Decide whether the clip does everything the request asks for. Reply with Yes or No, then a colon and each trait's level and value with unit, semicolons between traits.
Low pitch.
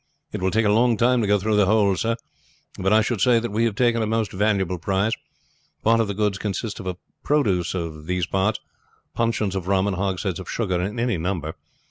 Yes: low, 100 Hz